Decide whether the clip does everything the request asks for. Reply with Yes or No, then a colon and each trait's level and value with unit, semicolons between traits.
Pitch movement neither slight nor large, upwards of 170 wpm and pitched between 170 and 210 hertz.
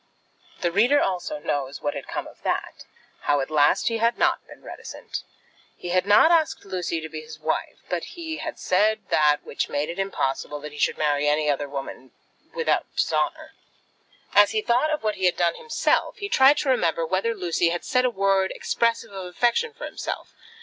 No: wide, 7.4 semitones; average, 200 wpm; high, 190 Hz